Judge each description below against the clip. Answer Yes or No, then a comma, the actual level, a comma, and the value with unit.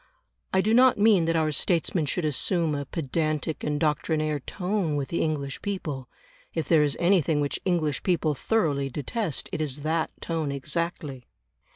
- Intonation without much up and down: No, average, 3.1 semitones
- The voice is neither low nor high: Yes, medium, 155 Hz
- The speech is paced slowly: No, average, 165 wpm